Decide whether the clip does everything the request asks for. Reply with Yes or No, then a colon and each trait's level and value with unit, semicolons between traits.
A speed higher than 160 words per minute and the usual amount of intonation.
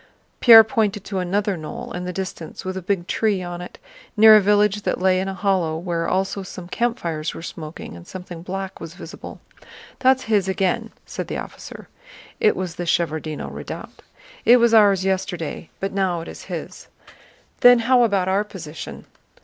Yes: average, 180 wpm; average, 3.0 semitones